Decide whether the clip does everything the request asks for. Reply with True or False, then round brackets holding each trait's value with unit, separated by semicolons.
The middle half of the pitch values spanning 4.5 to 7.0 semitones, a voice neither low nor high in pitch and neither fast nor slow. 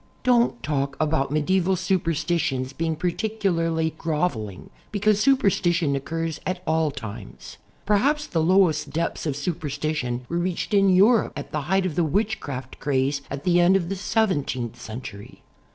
True (5.1 semitones; 165 Hz; 150 wpm)